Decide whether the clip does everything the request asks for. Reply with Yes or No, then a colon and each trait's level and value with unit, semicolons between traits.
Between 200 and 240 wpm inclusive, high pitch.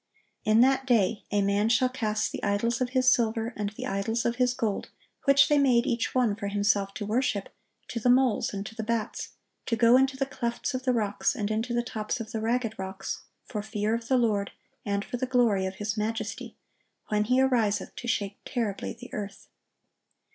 Yes: fast, 205 wpm; high, 225 Hz